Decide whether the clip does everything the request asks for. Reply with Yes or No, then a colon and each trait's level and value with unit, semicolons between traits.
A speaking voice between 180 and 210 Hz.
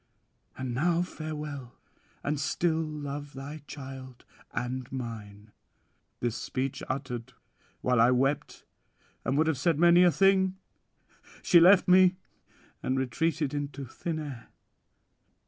No: medium, 145 Hz